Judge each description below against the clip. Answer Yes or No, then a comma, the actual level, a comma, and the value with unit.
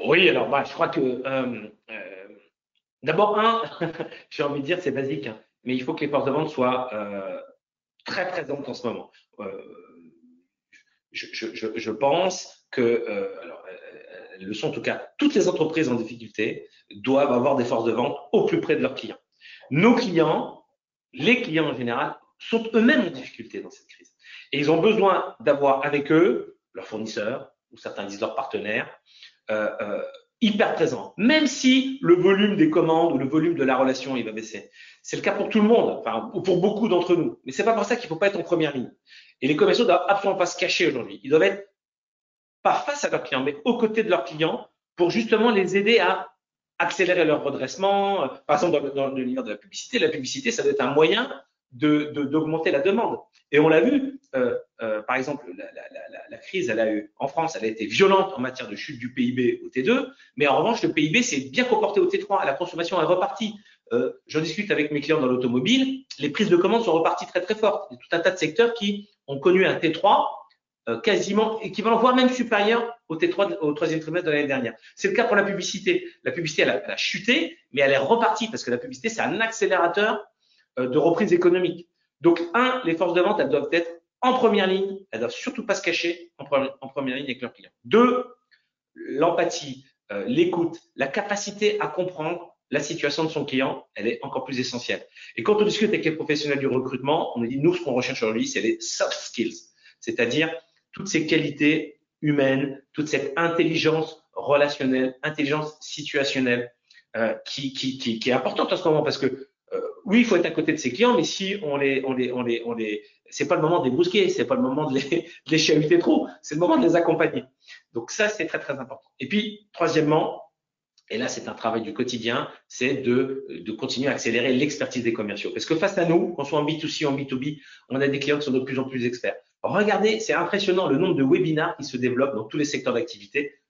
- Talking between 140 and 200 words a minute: No, fast, 220 wpm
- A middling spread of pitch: No, wide, 7.9 semitones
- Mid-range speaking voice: Yes, medium, 170 Hz